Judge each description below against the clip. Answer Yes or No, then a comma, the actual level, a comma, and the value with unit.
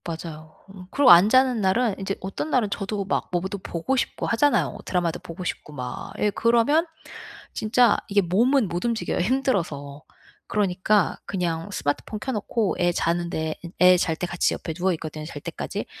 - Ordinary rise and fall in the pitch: Yes, average, 4.8 semitones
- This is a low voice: No, high, 190 Hz